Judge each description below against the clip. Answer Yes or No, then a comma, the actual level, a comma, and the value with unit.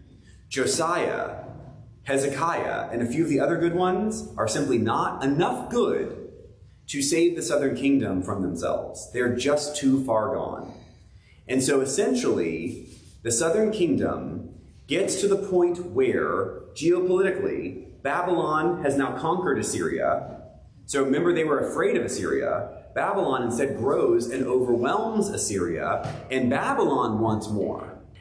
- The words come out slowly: Yes, slow, 130 wpm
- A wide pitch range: Yes, wide, 7.2 semitones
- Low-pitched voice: No, medium, 145 Hz